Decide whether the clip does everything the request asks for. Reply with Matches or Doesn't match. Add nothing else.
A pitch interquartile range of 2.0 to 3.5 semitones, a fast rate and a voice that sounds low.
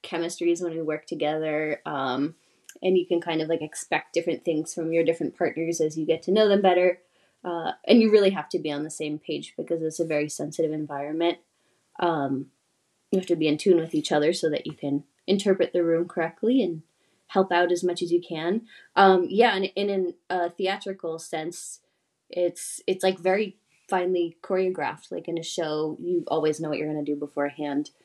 Doesn't match